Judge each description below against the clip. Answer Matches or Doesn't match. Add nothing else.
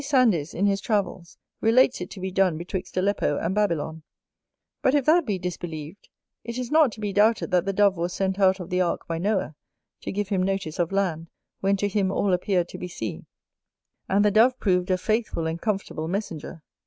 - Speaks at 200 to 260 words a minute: Matches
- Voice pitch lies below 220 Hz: Matches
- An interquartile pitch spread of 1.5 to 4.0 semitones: Matches